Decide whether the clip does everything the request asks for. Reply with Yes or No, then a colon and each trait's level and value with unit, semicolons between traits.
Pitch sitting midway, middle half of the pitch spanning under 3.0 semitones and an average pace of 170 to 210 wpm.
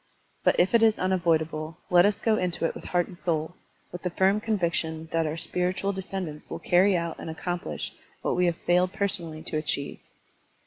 Yes: medium, 175 Hz; narrow, 2.5 semitones; average, 190 wpm